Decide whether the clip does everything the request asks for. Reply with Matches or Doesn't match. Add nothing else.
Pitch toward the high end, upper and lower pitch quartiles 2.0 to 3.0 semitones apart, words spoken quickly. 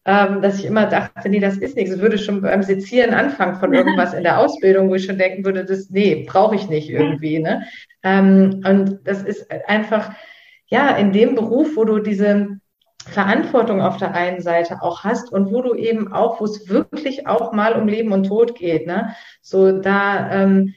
Matches